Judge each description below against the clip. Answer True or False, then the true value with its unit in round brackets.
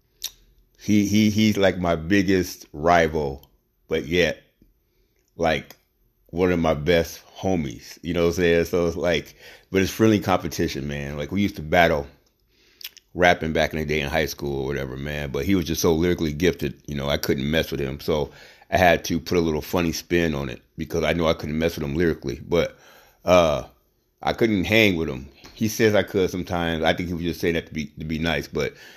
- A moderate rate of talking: False (215 wpm)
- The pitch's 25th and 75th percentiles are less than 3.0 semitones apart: False (3.3 semitones)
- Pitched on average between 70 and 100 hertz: True (85 Hz)